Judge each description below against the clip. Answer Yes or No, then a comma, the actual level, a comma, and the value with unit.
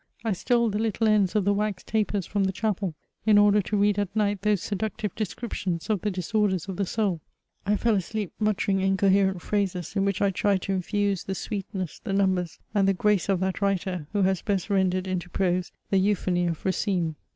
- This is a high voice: Yes, high, 195 Hz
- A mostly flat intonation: Yes, narrow, 1.9 semitones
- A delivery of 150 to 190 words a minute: No, fast, 205 wpm